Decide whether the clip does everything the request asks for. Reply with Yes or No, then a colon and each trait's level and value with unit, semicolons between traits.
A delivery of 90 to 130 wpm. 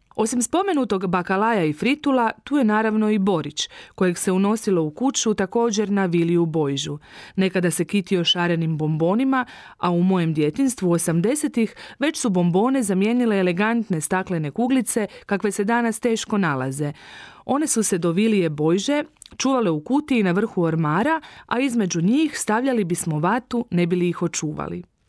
No: average, 150 wpm